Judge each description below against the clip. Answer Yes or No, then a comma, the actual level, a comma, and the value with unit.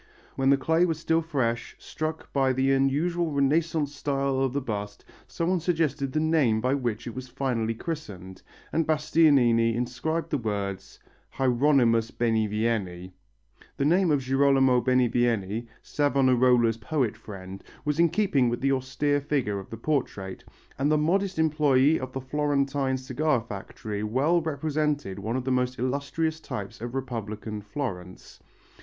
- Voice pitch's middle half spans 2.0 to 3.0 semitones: No, average, 4.5 semitones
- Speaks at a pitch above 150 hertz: No, low, 130 Hz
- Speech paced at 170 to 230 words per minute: No, average, 145 wpm